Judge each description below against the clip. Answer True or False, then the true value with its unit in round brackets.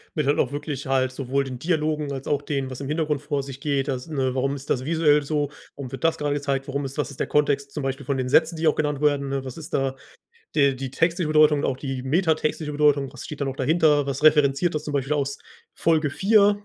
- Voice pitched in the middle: True (145 Hz)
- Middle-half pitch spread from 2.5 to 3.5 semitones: False (2.1 semitones)